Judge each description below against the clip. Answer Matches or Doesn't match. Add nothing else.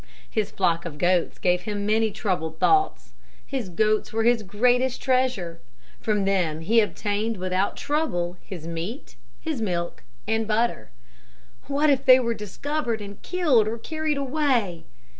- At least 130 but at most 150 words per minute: Matches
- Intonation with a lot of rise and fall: Matches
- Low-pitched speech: Doesn't match